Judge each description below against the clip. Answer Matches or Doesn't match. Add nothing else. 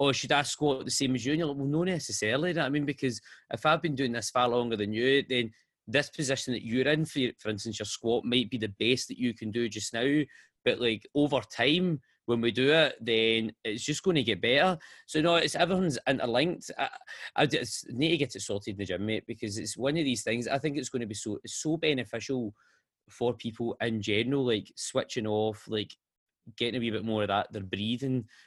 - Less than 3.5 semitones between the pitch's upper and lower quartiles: Doesn't match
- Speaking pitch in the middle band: Doesn't match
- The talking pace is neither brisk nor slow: Doesn't match